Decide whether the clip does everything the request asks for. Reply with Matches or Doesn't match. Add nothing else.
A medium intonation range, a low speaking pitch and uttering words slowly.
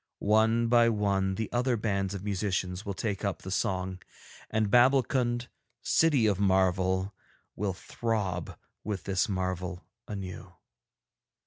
Matches